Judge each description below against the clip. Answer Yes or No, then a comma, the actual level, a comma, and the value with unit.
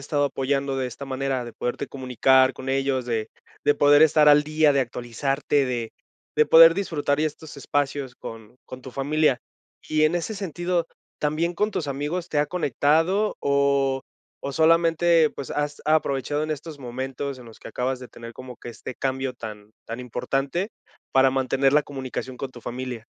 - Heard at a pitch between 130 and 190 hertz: Yes, medium, 140 Hz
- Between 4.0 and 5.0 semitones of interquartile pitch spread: No, average, 2.9 semitones